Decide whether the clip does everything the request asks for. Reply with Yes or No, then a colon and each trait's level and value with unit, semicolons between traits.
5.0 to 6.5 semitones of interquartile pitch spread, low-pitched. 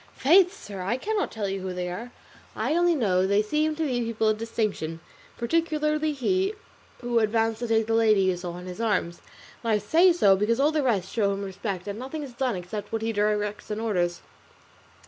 No: wide, 5.4 semitones; high, 225 Hz